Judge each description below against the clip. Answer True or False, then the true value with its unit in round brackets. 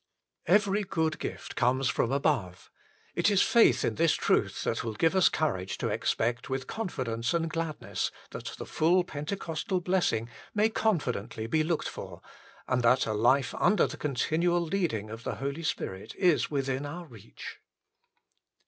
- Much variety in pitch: True (6.4 semitones)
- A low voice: False (150 Hz)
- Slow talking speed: False (160 wpm)